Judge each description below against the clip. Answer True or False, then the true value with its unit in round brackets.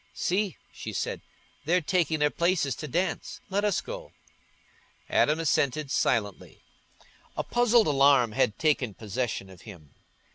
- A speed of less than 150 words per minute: True (135 wpm)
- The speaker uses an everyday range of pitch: False (7.0 semitones)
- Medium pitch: True (150 Hz)